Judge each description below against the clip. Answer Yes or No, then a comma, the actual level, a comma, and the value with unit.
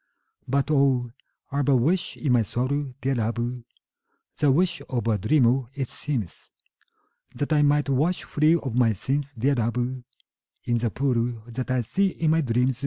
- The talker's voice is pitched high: No, low, 130 Hz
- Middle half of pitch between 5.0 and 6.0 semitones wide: No, average, 3.3 semitones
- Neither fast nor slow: Yes, average, 175 wpm